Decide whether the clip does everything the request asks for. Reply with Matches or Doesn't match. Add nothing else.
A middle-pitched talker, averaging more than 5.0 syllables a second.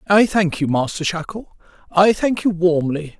Doesn't match